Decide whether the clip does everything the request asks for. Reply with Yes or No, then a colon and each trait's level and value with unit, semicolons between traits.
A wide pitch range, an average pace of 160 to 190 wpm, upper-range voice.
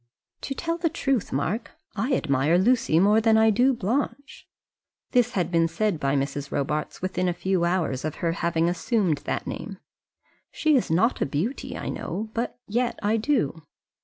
Yes: wide, 6.7 semitones; average, 170 wpm; high, 195 Hz